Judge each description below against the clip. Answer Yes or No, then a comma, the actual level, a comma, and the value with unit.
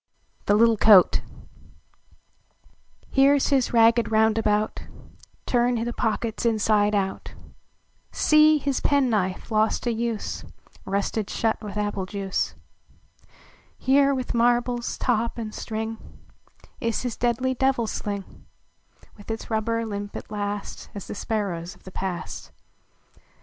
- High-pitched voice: Yes, high, 225 Hz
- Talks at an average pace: No, slow, 125 wpm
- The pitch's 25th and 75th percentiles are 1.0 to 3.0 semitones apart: Yes, narrow, 2.6 semitones